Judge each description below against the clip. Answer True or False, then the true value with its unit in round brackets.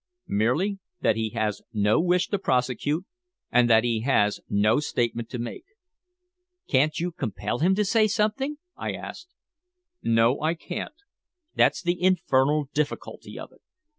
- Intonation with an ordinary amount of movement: False (8.0 semitones)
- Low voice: False (145 Hz)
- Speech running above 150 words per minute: False (145 wpm)